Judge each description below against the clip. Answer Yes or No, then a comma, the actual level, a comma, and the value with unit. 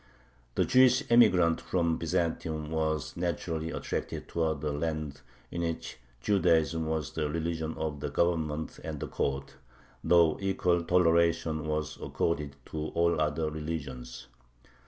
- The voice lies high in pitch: No, very low, 80 Hz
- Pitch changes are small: Yes, narrow, 1.8 semitones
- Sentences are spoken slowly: Yes, slow, 130 wpm